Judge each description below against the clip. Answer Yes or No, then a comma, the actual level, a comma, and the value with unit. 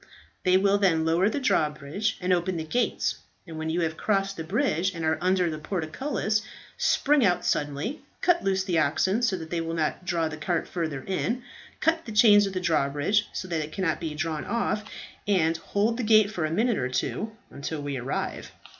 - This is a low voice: No, medium, 180 Hz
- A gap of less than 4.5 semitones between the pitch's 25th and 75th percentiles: No, average, 4.8 semitones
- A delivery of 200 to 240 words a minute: Yes, fast, 205 wpm